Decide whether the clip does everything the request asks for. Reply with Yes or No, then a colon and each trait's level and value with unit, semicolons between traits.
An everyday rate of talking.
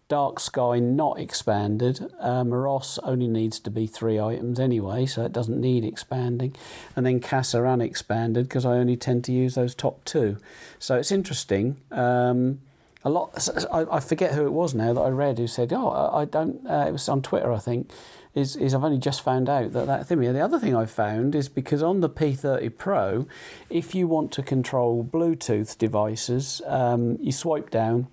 Yes: average, 195 wpm